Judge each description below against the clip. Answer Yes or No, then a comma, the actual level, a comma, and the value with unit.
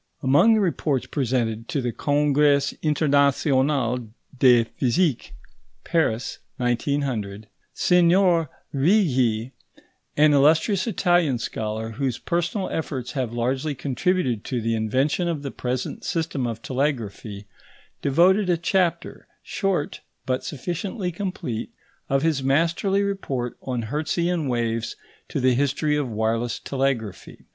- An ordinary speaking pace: No, slow, 115 wpm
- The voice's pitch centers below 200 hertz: Yes, medium, 140 Hz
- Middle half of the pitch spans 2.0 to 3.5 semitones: No, average, 5.3 semitones